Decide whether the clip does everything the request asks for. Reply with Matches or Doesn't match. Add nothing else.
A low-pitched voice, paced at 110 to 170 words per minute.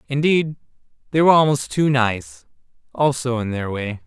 Matches